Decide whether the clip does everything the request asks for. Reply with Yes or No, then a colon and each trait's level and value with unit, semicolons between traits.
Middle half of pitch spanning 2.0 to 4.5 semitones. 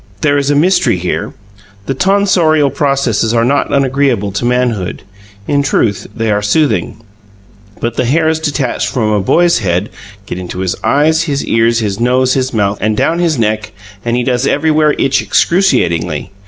No: wide, 5.5 semitones